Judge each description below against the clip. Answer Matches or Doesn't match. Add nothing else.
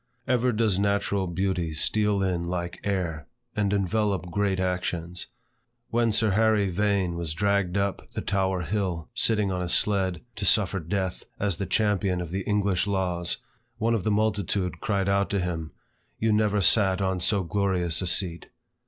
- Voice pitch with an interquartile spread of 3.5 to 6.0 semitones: Doesn't match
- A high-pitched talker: Doesn't match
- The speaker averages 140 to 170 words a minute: Matches